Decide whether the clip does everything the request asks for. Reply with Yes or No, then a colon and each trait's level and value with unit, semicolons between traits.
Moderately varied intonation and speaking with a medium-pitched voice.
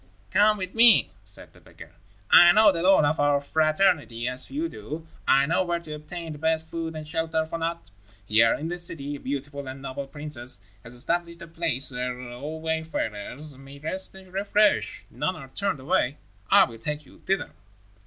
Yes: average, 4.0 semitones; medium, 155 Hz